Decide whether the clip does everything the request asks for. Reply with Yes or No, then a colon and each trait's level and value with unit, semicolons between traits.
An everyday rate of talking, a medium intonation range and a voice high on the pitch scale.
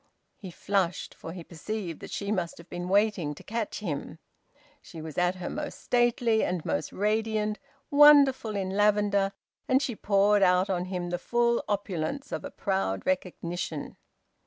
Yes: average, 160 wpm; average, 3.7 semitones; high, 195 Hz